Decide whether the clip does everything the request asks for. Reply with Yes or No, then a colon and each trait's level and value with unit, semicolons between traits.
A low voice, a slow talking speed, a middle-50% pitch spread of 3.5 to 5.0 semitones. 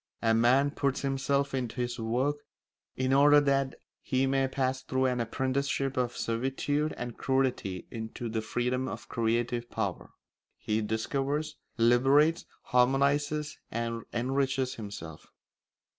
No: low, 130 Hz; slow, 125 wpm; average, 2.8 semitones